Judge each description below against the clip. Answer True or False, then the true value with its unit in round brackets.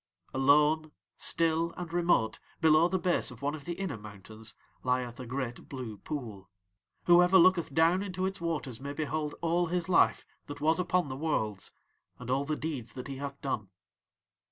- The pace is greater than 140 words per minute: True (175 wpm)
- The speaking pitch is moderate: True (150 Hz)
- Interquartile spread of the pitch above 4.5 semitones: True (4.9 semitones)